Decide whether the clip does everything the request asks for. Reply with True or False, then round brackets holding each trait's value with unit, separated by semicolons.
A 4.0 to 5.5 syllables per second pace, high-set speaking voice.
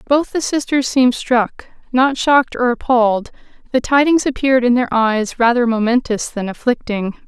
True (5.0 syllables/s; 245 Hz)